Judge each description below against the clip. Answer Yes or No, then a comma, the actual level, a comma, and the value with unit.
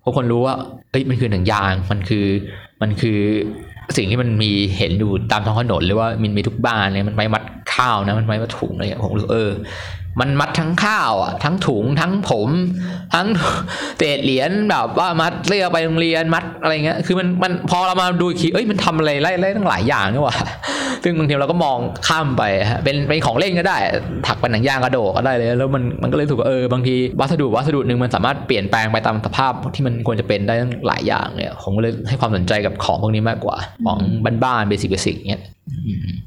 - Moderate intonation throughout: No, wide, 7.0 semitones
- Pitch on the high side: No, low, 125 Hz